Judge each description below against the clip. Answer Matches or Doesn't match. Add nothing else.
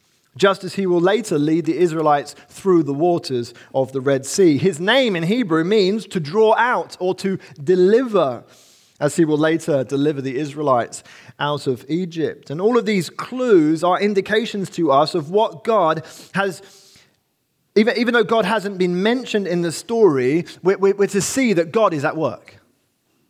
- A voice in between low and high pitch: Matches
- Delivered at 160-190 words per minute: Matches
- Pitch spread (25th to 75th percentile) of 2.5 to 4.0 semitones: Doesn't match